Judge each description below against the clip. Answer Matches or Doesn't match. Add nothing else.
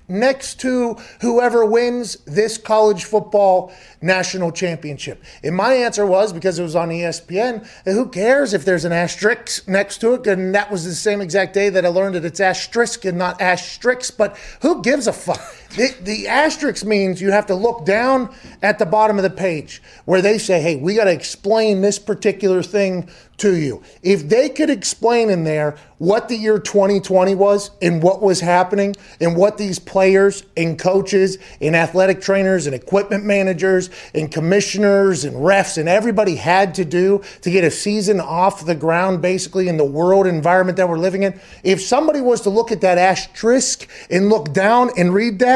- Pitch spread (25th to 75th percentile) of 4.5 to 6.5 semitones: Doesn't match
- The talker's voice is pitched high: Matches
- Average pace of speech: Matches